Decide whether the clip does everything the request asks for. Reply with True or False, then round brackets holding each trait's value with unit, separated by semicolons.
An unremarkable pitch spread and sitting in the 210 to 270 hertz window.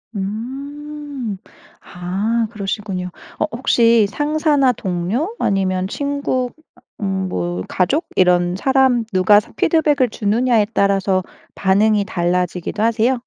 False (5.7 semitones; 215 Hz)